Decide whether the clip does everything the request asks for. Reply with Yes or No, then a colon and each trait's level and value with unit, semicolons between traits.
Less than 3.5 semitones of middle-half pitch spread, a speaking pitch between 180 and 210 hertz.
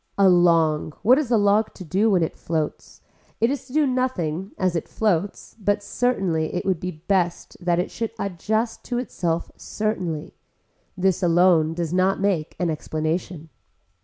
No: average, 4.3 semitones; medium, 185 Hz